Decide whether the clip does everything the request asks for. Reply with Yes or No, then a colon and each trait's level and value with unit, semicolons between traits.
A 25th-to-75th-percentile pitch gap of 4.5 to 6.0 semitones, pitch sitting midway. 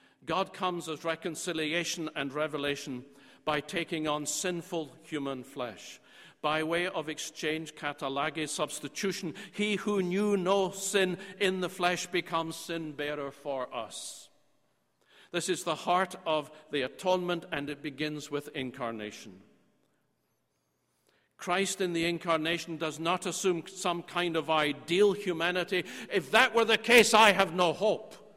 No: average, 3.5 semitones; medium, 165 Hz